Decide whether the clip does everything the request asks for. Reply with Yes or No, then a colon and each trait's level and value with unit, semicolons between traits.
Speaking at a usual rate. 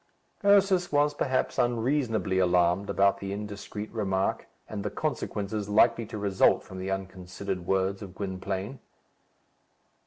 No: slow, 125 wpm